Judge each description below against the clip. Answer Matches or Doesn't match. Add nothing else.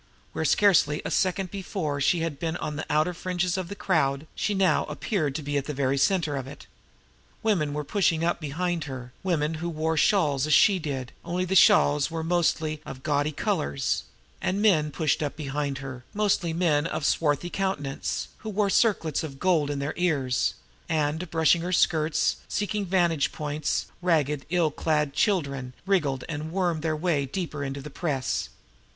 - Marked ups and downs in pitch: Doesn't match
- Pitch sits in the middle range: Matches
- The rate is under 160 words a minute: Doesn't match